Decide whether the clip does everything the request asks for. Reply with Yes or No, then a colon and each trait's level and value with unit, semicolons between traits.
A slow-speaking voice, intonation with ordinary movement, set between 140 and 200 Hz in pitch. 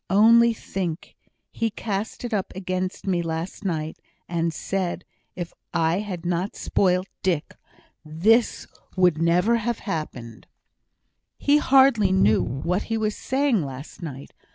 Yes: slow, 130 wpm; average, 4.5 semitones; medium, 185 Hz